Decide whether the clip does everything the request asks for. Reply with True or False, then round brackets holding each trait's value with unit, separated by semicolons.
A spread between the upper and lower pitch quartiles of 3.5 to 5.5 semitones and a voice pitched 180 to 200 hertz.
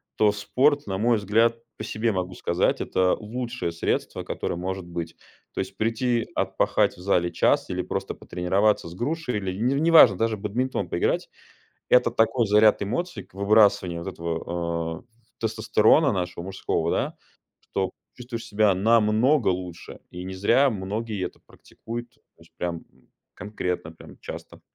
False (4.2 semitones; 105 Hz)